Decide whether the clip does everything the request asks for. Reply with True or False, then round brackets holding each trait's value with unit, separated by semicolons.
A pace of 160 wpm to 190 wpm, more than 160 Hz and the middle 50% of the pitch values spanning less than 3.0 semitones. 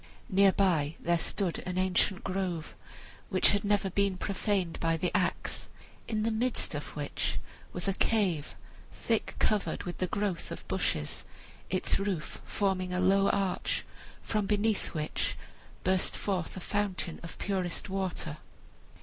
False (145 wpm; 190 Hz; 2.4 semitones)